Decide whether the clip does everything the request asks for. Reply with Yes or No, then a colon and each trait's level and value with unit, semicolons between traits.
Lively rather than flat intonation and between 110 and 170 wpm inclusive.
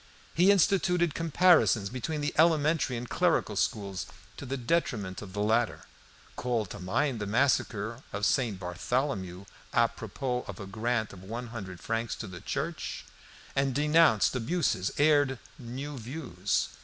Yes: wide, 6.0 semitones; average, 145 wpm